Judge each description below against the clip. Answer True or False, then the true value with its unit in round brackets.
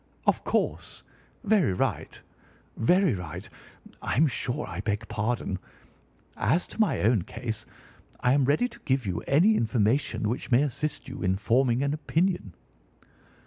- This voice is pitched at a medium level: False (125 Hz)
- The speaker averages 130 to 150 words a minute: True (145 wpm)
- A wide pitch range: True (5.9 semitones)